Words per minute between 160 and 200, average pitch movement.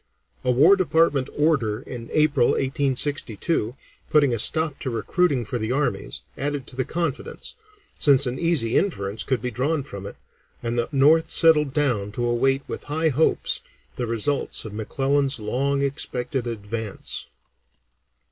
No: average, 145 wpm; average, 3.8 semitones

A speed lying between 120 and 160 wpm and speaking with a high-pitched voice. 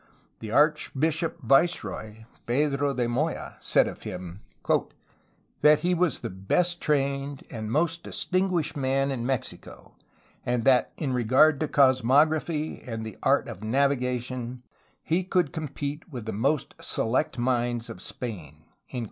No: average, 140 wpm; low, 135 Hz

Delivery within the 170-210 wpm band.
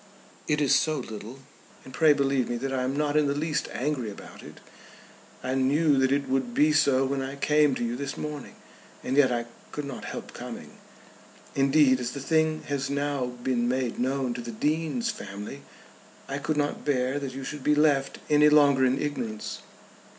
Yes: average, 195 wpm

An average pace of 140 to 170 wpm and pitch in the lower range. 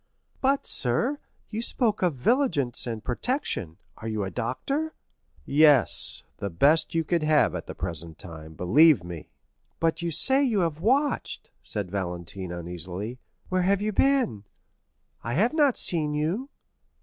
No: average, 145 wpm; medium, 150 Hz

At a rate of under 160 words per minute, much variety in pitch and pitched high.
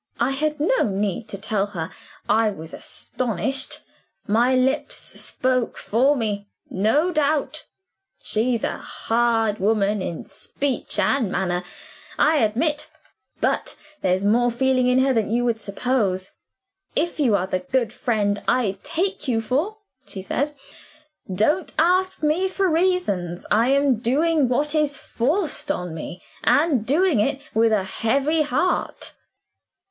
Yes: average, 140 wpm; wide, 6.1 semitones; high, 245 Hz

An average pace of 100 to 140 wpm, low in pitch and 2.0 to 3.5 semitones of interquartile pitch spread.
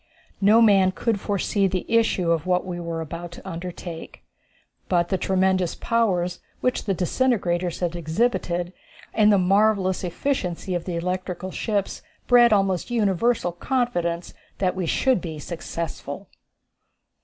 No: slow, 135 wpm; medium, 185 Hz; average, 3.2 semitones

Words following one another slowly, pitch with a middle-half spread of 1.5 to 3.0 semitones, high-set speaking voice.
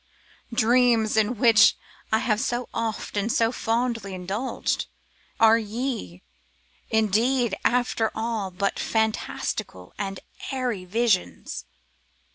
Yes: slow, 105 wpm; narrow, 2.6 semitones; high, 225 Hz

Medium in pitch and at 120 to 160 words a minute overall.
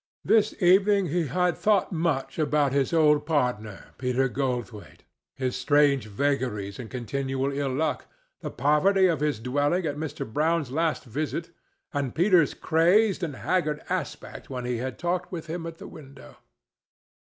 Yes: medium, 145 Hz; average, 150 wpm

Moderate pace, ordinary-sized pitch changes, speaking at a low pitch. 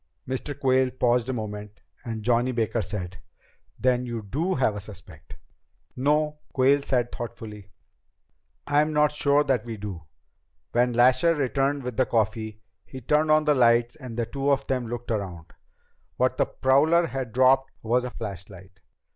Yes: average, 160 wpm; average, 3.8 semitones; low, 125 Hz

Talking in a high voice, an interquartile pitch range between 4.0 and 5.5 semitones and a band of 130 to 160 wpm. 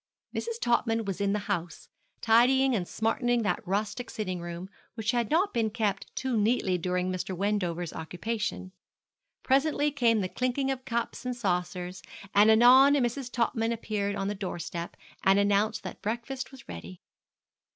Yes: high, 215 Hz; average, 4.5 semitones; average, 155 wpm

